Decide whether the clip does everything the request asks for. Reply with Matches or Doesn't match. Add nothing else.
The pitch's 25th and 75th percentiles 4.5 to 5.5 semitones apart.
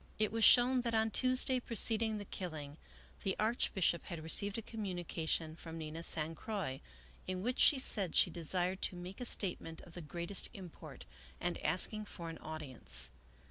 Matches